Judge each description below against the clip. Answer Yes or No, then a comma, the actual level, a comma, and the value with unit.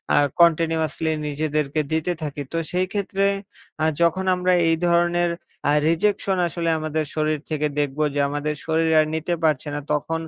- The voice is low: No, medium, 160 Hz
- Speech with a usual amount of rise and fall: No, narrow, 2.1 semitones